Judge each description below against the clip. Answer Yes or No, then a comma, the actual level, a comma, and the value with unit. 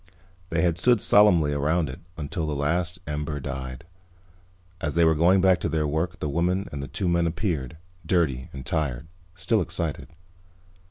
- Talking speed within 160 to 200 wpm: Yes, average, 170 wpm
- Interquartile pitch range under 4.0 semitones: Yes, average, 3.4 semitones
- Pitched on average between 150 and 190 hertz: No, very low, 80 Hz